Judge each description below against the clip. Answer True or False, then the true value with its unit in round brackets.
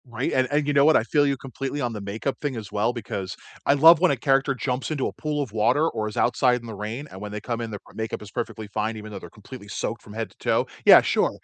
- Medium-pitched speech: False (120 Hz)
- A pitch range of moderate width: True (4.4 semitones)